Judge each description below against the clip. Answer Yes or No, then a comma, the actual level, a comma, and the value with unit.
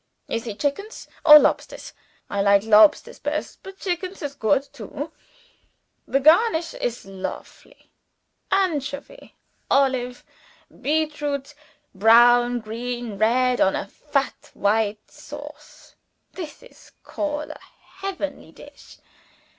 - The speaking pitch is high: Yes, very high, 275 Hz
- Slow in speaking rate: Yes, slow, 105 wpm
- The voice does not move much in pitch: No, average, 5.3 semitones